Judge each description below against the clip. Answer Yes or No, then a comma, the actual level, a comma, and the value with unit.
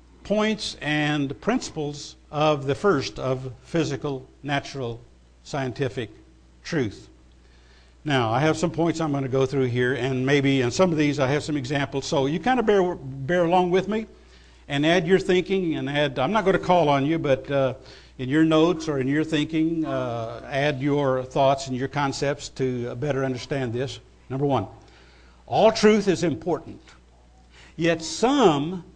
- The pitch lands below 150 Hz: Yes, medium, 140 Hz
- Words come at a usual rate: Yes, average, 170 wpm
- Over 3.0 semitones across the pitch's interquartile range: Yes, average, 3.9 semitones